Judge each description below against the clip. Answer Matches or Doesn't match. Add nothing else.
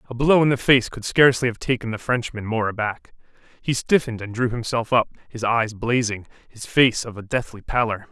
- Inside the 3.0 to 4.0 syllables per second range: Doesn't match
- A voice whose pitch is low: Matches